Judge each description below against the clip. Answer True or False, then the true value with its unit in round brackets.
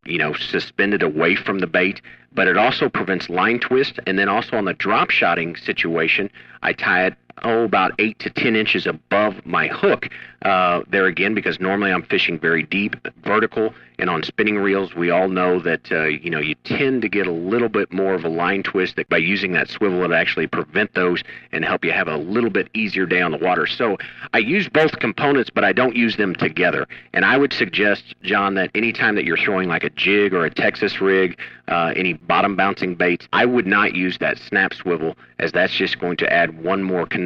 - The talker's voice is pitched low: True (95 Hz)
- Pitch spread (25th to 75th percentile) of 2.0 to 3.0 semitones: False (3.6 semitones)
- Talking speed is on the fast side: True (220 wpm)